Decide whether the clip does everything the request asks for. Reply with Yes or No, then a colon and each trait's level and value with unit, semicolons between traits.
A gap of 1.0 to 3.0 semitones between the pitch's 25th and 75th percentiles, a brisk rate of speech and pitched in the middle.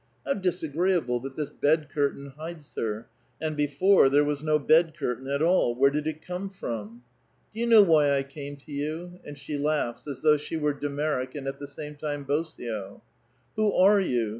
Yes: narrow, 2.6 semitones; fast, 215 wpm; medium, 145 Hz